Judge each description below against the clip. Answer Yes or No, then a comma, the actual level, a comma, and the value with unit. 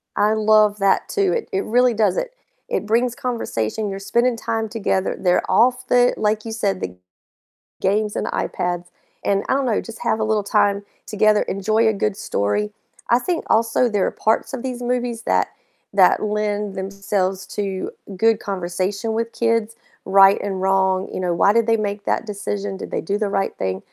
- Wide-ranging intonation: No, average, 2.7 semitones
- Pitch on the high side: Yes, high, 210 Hz